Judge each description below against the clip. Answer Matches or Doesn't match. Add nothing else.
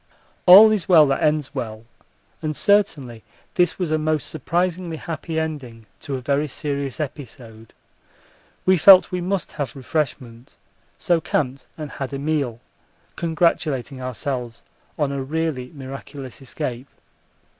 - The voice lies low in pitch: Doesn't match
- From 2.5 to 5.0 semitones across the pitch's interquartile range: Matches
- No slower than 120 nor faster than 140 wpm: Matches